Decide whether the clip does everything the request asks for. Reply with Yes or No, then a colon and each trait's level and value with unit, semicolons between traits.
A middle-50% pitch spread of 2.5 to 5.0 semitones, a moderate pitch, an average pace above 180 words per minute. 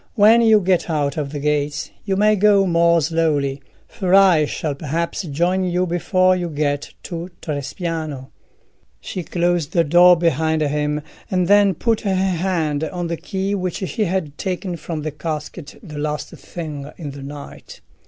No: average, 3.7 semitones; medium, 170 Hz; average, 165 wpm